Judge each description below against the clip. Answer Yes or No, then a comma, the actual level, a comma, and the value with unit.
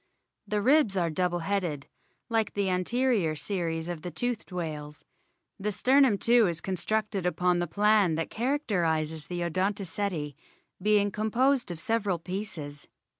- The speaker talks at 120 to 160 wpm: Yes, average, 145 wpm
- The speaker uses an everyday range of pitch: Yes, average, 4.3 semitones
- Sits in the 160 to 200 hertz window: Yes, medium, 185 Hz